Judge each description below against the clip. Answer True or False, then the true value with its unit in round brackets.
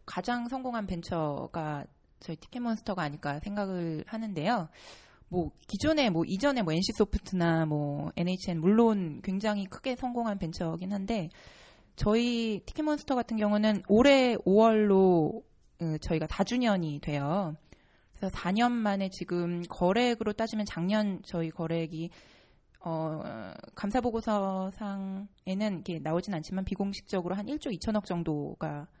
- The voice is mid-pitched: False (195 Hz)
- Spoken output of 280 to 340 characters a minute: True (290 characters per minute)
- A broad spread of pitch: False (4.7 semitones)